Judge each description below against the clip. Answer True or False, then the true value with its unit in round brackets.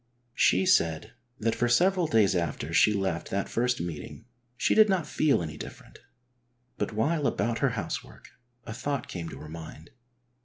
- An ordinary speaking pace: True (165 wpm)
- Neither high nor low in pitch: False (110 Hz)